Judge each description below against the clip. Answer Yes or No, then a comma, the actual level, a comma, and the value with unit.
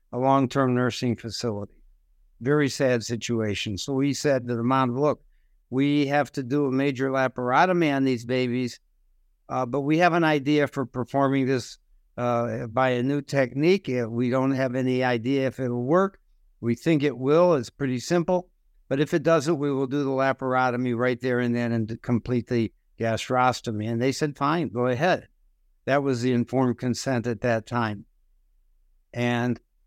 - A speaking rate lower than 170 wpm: No, average, 175 wpm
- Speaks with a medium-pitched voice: No, low, 125 Hz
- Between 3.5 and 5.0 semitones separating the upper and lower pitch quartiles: No, average, 2.8 semitones